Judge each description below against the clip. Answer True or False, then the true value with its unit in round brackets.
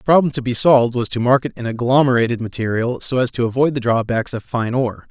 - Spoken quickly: True (235 wpm)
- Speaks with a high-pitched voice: False (125 Hz)